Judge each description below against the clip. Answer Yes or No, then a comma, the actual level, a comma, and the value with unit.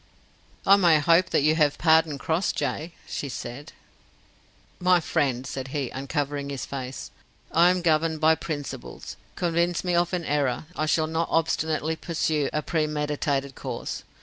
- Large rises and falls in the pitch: No, average, 2.8 semitones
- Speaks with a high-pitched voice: No, medium, 155 Hz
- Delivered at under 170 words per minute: Yes, average, 150 wpm